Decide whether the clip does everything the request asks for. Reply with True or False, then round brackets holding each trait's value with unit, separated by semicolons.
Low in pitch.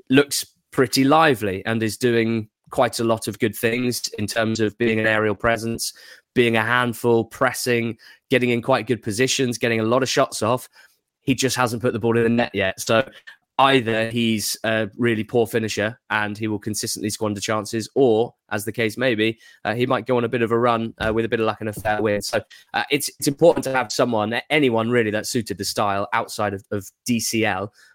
True (115 Hz)